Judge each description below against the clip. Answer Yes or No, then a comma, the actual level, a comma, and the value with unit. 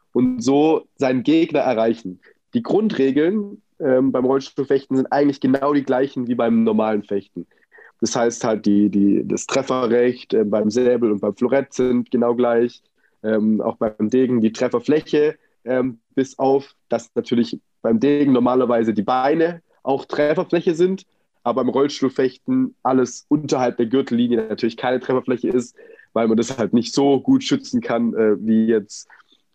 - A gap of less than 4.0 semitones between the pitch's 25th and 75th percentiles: Yes, average, 3.5 semitones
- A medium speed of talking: Yes, average, 155 wpm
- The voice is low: Yes, low, 130 Hz